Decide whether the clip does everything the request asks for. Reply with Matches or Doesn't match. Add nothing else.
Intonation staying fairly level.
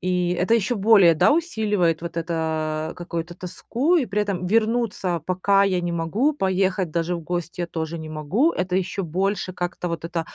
Doesn't match